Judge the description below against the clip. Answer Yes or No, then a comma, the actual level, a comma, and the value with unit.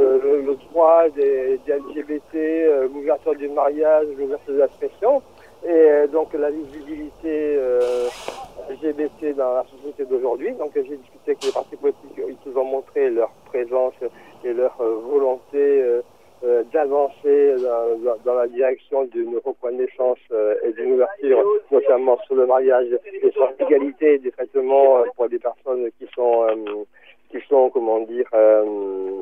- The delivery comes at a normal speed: Yes, average, 160 wpm